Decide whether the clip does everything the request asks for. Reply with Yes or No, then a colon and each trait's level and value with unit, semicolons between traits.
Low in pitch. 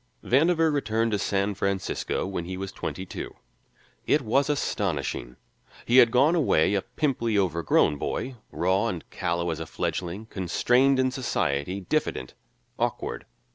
Yes: low, 100 Hz